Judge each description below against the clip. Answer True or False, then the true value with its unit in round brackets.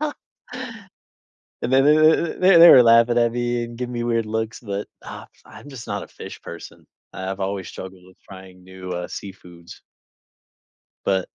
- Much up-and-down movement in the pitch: True (5.8 semitones)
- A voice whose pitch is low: True (115 Hz)